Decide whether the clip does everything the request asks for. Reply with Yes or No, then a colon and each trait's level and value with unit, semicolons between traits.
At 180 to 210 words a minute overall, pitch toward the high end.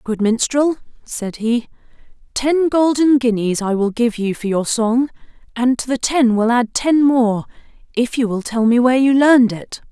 Yes: average, 190 wpm; high, 245 Hz